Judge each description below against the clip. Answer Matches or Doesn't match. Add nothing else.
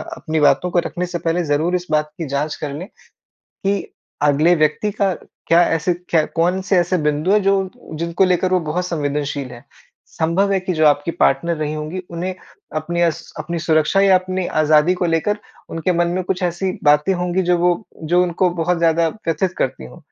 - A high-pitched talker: Doesn't match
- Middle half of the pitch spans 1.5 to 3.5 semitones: Matches